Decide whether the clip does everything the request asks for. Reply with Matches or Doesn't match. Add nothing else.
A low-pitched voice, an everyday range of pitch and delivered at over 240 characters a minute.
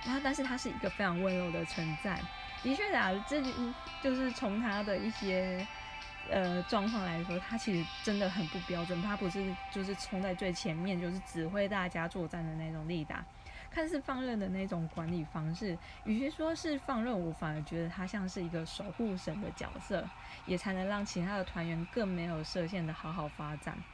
Doesn't match